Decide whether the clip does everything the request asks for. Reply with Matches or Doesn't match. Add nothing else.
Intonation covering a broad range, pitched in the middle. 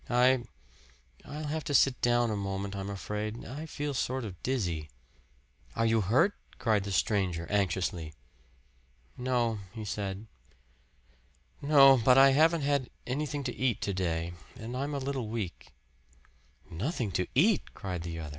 Doesn't match